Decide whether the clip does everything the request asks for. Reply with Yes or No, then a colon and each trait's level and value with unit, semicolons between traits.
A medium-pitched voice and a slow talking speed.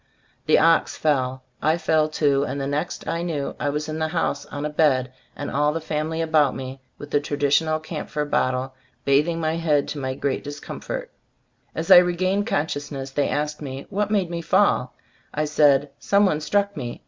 No: medium, 150 Hz; average, 190 wpm